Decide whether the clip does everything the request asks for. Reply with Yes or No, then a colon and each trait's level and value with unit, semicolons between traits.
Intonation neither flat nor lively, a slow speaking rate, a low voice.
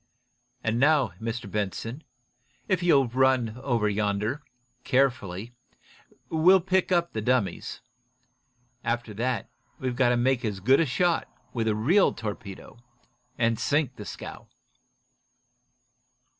Yes: average, 4.2 semitones; slow, 120 wpm; low, 120 Hz